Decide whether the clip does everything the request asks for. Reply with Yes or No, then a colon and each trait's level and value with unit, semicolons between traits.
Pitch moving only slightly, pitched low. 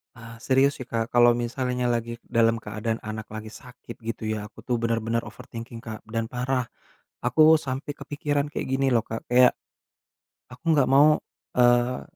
Yes: narrow, 2.1 semitones; low, 120 Hz